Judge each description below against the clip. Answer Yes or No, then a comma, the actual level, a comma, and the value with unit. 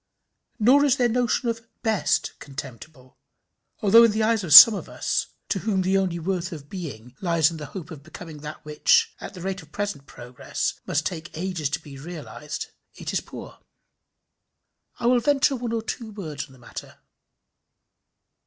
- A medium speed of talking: Yes, average, 180 wpm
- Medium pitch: Yes, medium, 180 Hz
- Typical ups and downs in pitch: No, wide, 6.6 semitones